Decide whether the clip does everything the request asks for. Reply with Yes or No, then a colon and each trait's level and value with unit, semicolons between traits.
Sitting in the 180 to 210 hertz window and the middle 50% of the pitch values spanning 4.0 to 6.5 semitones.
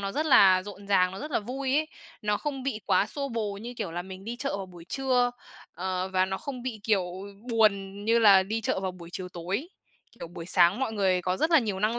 Yes: high, 205 Hz; average, 4.6 semitones